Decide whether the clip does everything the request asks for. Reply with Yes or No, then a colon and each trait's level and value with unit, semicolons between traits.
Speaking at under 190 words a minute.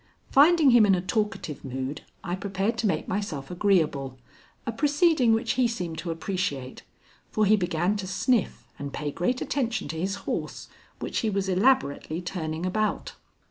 Yes: average, 165 wpm